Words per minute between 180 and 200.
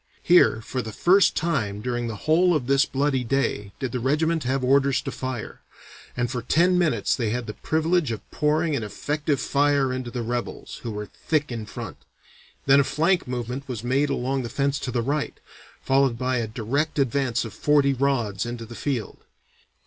Yes: average, 190 wpm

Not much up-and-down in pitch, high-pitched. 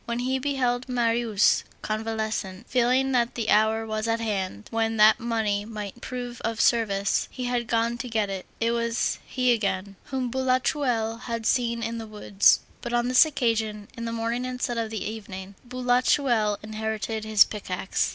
Yes: narrow, 2.2 semitones; high, 230 Hz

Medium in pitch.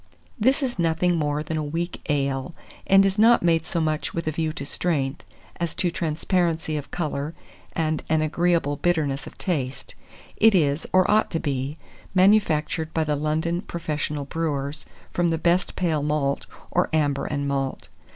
Yes: medium, 160 Hz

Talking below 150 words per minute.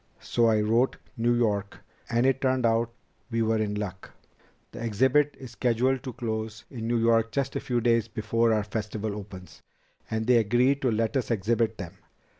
No: average, 185 wpm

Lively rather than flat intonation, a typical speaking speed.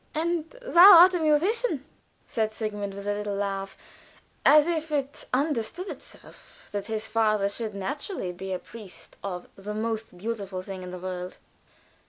Yes: wide, 7.4 semitones; average, 160 wpm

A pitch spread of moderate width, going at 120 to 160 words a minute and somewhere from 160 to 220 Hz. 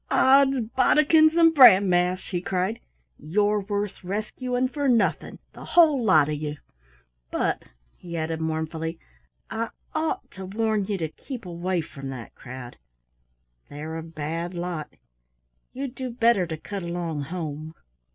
No: wide, 6.7 semitones; average, 140 wpm; medium, 185 Hz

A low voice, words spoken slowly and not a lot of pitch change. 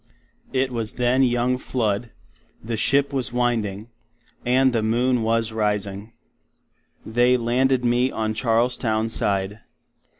Yes: low, 120 Hz; slow, 120 wpm; narrow, 2.3 semitones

